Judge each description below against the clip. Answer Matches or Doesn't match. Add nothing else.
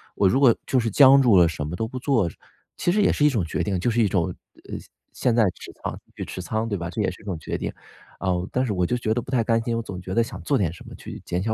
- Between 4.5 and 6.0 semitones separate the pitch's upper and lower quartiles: Matches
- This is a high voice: Doesn't match